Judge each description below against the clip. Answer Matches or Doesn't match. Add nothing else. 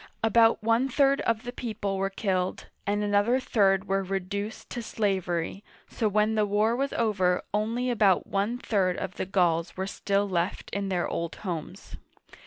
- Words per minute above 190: Doesn't match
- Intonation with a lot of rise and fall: Doesn't match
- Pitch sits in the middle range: Doesn't match